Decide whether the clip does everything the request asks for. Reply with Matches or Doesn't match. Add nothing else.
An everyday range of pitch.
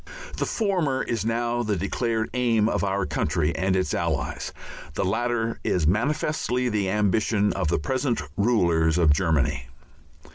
Matches